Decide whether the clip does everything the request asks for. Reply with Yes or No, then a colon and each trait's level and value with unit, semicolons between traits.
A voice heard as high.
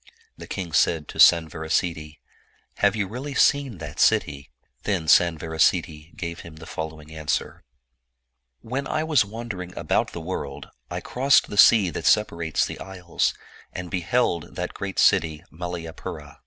No: very low, 85 Hz